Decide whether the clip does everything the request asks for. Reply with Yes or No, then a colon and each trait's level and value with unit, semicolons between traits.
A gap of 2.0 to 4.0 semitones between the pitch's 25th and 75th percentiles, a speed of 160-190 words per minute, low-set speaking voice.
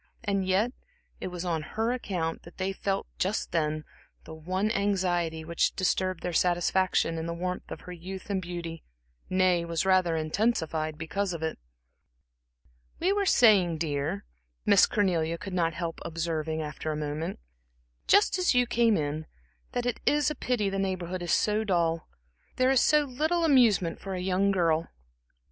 No: average, 3.7 semitones; average, 165 wpm; medium, 180 Hz